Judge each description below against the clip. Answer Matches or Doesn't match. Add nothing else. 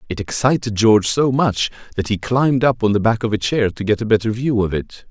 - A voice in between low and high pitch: Doesn't match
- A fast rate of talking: Matches